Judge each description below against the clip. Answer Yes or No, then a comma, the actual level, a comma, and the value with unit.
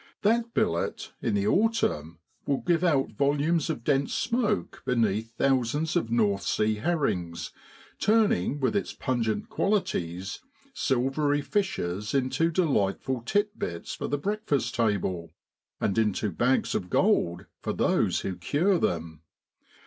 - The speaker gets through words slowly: Yes, slow, 130 wpm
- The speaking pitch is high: No, low, 130 Hz